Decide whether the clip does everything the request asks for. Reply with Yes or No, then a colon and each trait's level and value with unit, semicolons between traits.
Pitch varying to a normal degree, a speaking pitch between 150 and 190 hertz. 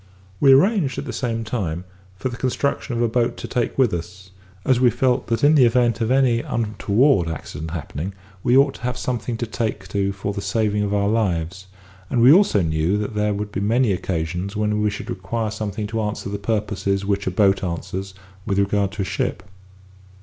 No: average, 3.6 semitones; low, 105 Hz